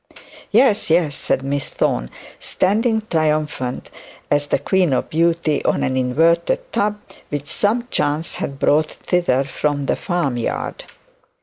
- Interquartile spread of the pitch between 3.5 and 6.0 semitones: Yes, average, 4.7 semitones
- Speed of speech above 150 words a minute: No, slow, 135 wpm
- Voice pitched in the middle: Yes, medium, 155 Hz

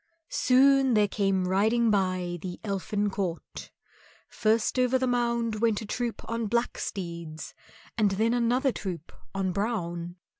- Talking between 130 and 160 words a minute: Yes, average, 140 wpm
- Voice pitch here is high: Yes, high, 210 Hz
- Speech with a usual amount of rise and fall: Yes, average, 4.1 semitones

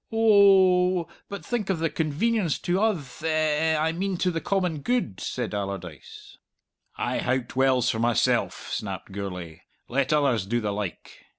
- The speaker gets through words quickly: No, average, 165 wpm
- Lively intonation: Yes, wide, 7.8 semitones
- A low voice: No, medium, 155 Hz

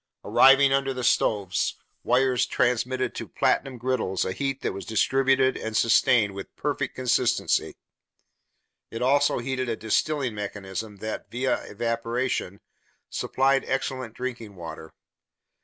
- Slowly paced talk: Yes, slow, 125 wpm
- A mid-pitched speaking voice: No, low, 125 Hz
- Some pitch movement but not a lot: Yes, average, 3.4 semitones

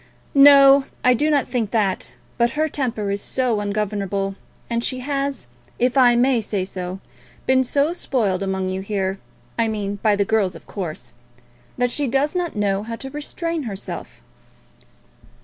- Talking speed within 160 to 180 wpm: Yes, average, 165 wpm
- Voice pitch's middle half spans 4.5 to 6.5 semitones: Yes, average, 5.3 semitones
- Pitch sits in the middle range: No, high, 230 Hz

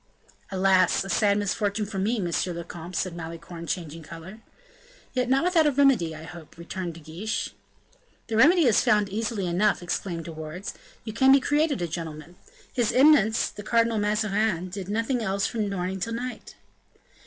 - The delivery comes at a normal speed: Yes, average, 170 wpm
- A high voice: Yes, high, 200 Hz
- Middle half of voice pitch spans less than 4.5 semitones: No, average, 4.8 semitones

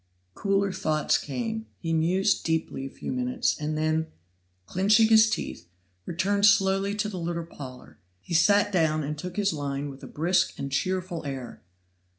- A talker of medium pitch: Yes, medium, 170 Hz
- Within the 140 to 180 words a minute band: Yes, average, 160 wpm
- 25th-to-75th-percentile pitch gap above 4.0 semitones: Yes, average, 4.7 semitones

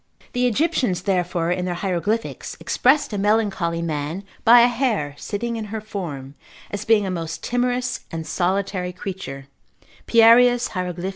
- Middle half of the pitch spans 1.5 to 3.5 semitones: No, average, 4.8 semitones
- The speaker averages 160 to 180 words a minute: No, average, 145 wpm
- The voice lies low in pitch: No, high, 195 Hz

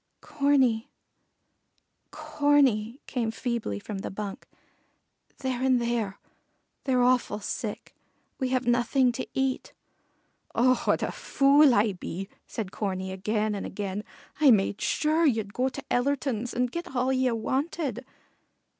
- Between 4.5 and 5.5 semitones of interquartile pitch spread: No, average, 4.0 semitones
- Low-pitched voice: No, high, 245 Hz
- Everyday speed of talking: No, slow, 130 wpm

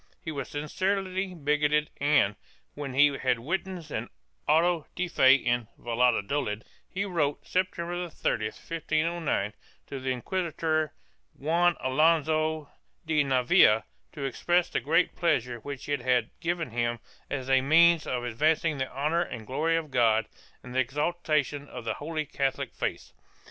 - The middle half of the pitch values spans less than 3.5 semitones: No, average, 4.3 semitones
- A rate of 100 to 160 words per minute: Yes, average, 145 wpm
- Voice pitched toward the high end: No, medium, 150 Hz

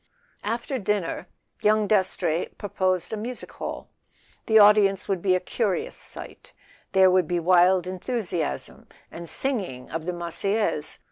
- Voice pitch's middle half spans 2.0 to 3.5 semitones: Yes, average, 3.1 semitones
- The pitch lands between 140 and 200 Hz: Yes, high, 190 Hz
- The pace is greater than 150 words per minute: No, slow, 135 wpm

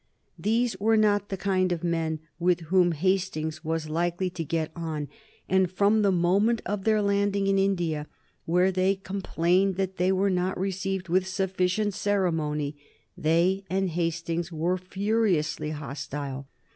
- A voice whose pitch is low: No, medium, 185 Hz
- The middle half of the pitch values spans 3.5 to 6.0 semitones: No, average, 2.9 semitones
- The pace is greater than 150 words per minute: No, average, 145 wpm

